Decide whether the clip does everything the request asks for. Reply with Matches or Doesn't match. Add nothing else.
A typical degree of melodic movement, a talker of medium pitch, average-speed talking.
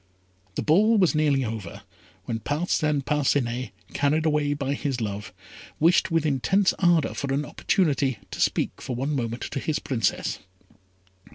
Matches